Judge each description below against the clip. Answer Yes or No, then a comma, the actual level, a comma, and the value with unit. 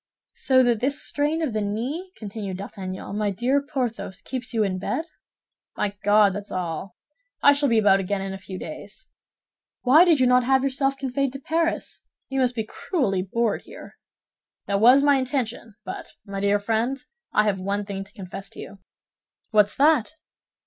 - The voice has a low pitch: No, high, 225 Hz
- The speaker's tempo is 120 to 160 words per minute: No, average, 180 wpm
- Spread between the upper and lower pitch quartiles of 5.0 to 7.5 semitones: Yes, average, 5.3 semitones